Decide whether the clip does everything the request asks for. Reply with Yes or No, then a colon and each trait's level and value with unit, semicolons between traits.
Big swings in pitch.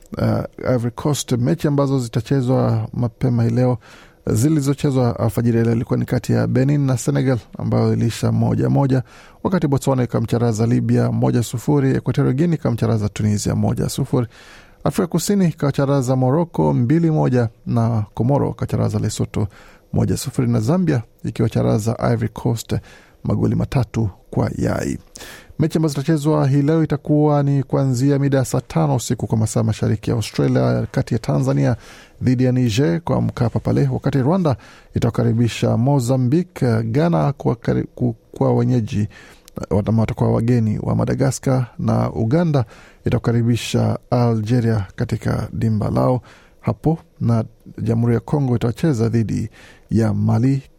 No: average, 3.6 semitones